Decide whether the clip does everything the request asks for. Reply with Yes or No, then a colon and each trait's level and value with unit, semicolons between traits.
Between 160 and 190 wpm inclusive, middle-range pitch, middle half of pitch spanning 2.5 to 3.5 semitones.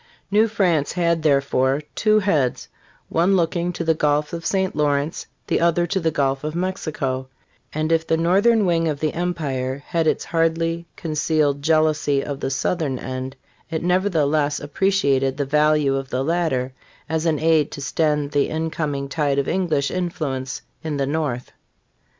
Yes: average, 165 wpm; medium, 155 Hz; average, 3.1 semitones